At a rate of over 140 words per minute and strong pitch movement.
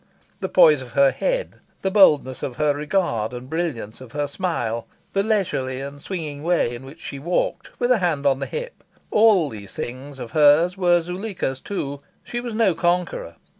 Yes: average, 185 wpm; wide, 6.0 semitones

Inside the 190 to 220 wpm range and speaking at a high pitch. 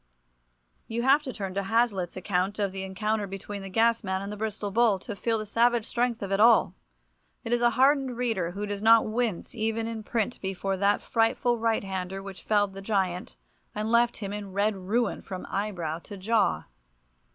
Yes: average, 195 wpm; high, 210 Hz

